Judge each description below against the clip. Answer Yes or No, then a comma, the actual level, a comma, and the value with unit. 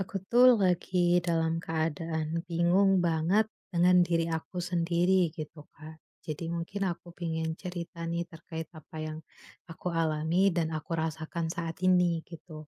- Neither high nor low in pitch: Yes, medium, 170 Hz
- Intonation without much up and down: Yes, narrow, 1.7 semitones